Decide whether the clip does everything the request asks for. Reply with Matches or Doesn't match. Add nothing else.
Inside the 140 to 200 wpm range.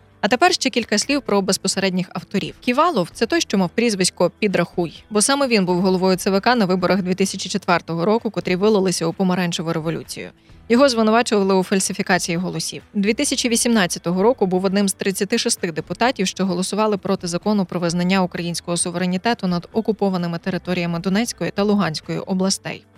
Matches